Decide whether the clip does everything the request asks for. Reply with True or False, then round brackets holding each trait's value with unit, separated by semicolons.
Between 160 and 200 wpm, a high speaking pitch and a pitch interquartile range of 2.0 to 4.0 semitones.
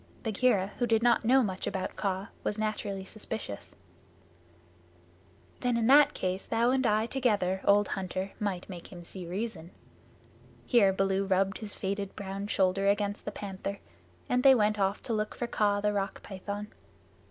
True (165 wpm; 205 Hz; 2.5 semitones)